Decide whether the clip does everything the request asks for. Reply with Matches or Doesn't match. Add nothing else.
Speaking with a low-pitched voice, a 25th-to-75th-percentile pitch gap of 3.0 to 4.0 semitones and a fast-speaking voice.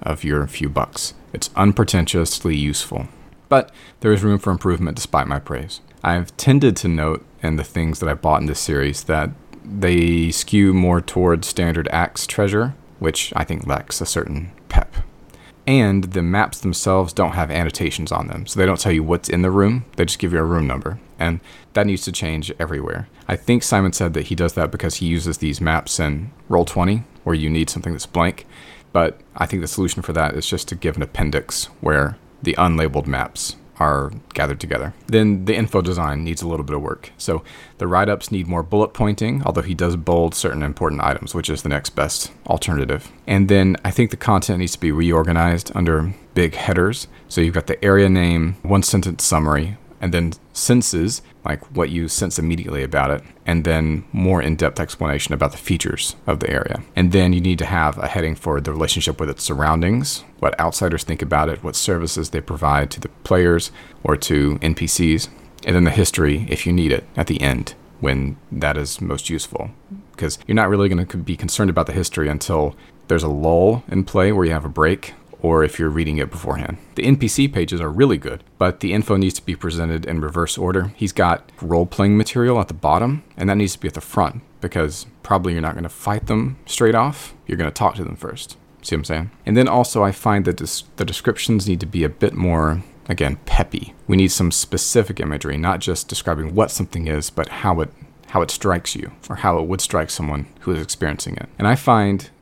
Matches